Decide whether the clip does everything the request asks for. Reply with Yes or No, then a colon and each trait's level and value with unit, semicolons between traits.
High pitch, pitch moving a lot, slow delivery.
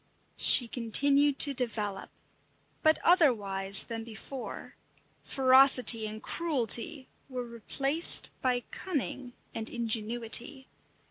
No: high, 245 Hz; average, 3.5 semitones; slow, 90 wpm